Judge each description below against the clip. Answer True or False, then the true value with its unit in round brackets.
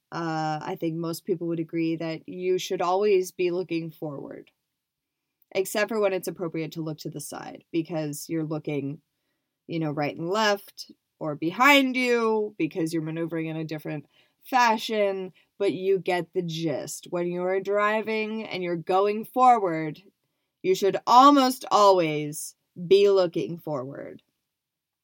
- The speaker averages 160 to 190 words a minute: False (145 wpm)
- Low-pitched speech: False (170 Hz)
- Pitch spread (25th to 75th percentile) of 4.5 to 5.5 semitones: False (3.9 semitones)